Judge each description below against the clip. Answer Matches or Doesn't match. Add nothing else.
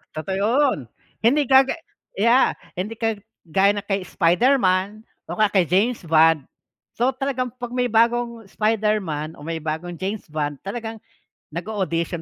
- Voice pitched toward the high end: Matches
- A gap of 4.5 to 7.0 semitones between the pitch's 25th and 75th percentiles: Matches